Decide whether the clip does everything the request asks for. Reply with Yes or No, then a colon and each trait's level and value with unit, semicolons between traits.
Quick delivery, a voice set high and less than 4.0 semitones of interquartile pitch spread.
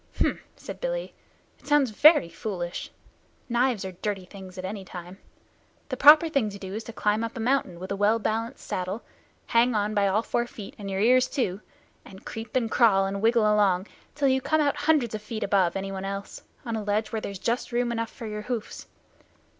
Yes: fast, 210 wpm; high, 215 Hz; average, 3.6 semitones